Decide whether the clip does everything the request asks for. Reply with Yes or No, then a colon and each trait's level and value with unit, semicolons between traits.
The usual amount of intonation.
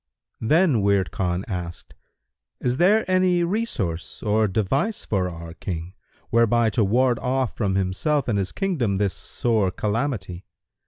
No: wide, 6.2 semitones